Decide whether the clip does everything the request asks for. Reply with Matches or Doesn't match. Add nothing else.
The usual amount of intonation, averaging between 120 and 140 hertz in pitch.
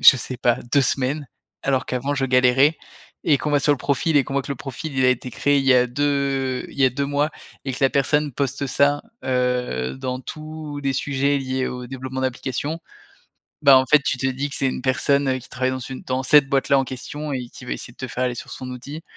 Doesn't match